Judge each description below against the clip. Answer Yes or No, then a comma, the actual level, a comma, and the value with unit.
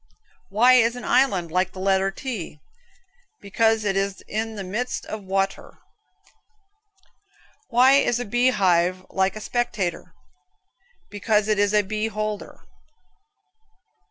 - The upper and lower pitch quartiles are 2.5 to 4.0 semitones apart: Yes, average, 2.8 semitones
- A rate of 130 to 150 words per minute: Yes, slow, 135 wpm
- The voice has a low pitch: No, high, 205 Hz